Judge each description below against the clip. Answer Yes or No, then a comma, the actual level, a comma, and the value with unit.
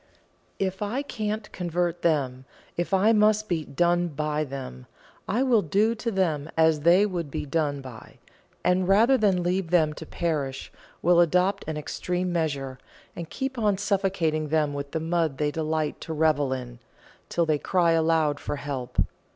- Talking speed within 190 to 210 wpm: No, average, 165 wpm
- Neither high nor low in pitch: Yes, medium, 165 Hz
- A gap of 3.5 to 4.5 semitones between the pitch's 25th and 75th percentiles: Yes, average, 4.2 semitones